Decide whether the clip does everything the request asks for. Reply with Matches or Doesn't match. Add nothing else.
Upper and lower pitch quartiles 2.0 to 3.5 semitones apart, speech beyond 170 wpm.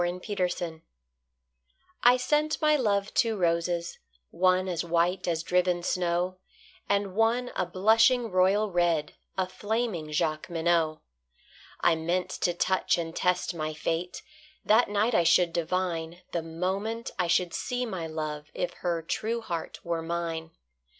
Doesn't match